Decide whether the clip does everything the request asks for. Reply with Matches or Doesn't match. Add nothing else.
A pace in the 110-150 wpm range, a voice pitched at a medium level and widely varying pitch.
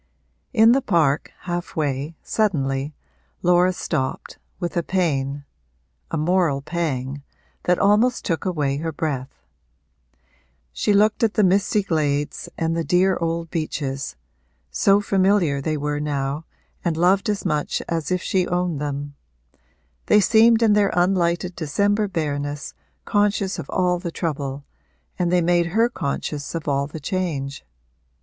Doesn't match